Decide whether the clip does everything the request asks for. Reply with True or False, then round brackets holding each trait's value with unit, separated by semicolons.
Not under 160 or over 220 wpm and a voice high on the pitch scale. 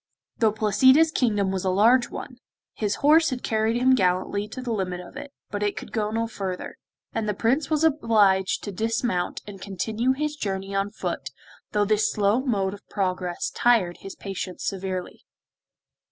True (175 wpm; 210 Hz)